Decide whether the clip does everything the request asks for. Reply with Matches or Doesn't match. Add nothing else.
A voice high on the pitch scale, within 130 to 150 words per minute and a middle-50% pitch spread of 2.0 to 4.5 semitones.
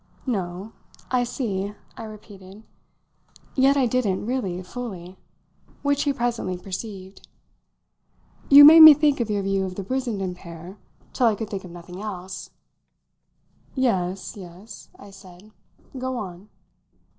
Doesn't match